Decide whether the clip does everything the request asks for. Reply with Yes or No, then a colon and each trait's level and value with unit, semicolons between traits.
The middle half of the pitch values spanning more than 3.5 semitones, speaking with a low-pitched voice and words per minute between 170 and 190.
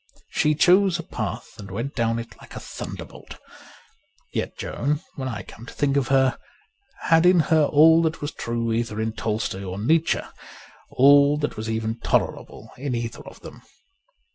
Yes: average, 5.0 semitones; low, 130 Hz; average, 175 wpm